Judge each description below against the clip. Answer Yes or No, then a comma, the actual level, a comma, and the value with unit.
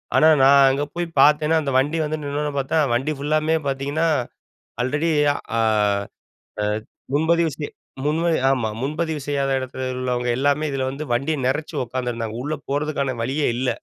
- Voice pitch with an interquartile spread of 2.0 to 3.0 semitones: Yes, narrow, 2.6 semitones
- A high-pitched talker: No, medium, 145 Hz